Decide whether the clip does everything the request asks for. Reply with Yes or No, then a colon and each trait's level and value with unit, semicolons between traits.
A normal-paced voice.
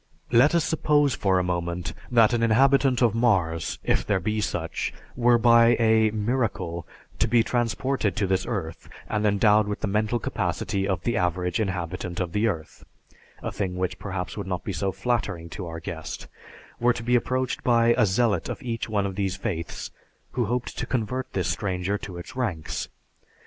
Yes: average, 185 wpm